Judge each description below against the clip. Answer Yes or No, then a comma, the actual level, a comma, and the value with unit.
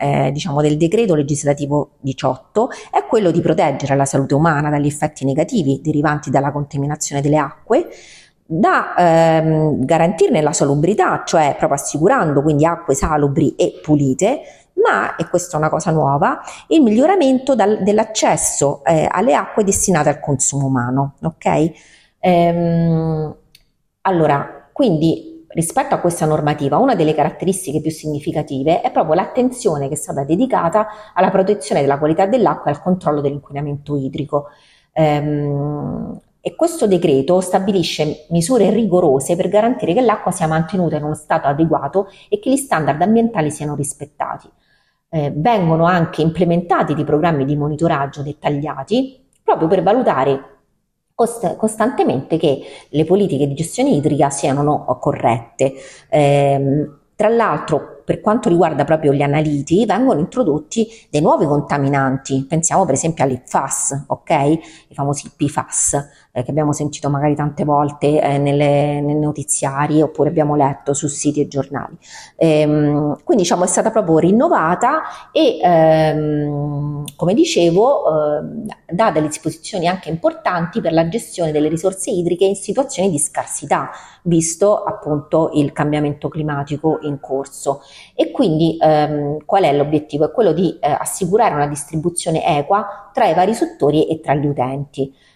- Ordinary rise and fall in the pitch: Yes, average, 3.6 semitones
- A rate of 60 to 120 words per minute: No, average, 140 wpm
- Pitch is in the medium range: Yes, medium, 155 Hz